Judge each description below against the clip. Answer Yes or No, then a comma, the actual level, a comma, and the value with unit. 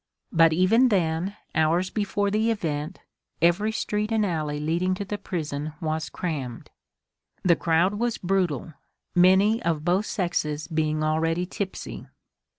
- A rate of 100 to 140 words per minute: Yes, slow, 135 wpm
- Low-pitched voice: No, medium, 175 Hz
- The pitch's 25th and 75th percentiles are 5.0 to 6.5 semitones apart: No, average, 4.2 semitones